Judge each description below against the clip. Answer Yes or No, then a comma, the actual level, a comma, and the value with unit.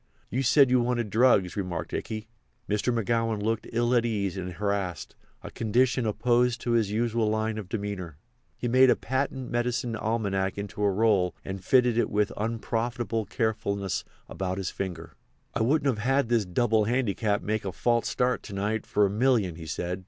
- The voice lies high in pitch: No, low, 110 Hz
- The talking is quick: No, average, 175 wpm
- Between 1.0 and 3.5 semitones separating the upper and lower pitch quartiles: Yes, average, 3.1 semitones